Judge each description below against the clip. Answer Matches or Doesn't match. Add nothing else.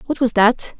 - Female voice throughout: Matches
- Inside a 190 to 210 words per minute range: Doesn't match